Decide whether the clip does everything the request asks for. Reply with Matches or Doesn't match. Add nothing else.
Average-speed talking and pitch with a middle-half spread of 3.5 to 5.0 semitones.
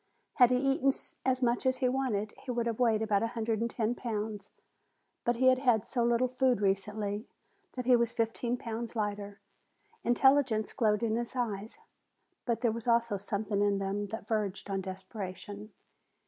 Doesn't match